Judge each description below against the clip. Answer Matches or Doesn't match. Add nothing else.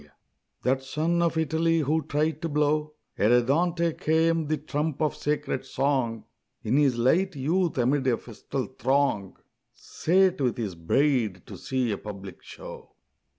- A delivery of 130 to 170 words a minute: Matches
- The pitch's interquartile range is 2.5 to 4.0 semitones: Doesn't match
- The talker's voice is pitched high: Doesn't match